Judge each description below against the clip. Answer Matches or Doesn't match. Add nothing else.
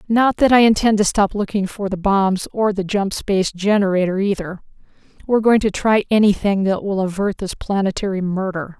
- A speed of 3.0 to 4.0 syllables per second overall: Doesn't match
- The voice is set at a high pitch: Matches